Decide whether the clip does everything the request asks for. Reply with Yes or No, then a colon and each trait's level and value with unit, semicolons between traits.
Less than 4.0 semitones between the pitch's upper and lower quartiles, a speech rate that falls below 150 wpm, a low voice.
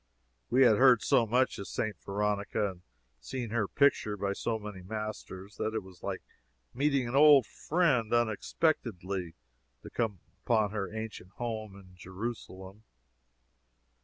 Yes: average, 3.4 semitones; average, 140 wpm; low, 110 Hz